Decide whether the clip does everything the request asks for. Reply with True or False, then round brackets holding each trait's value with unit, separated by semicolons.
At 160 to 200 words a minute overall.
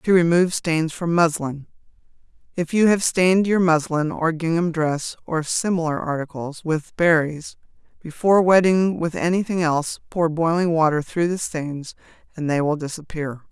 False (145 wpm)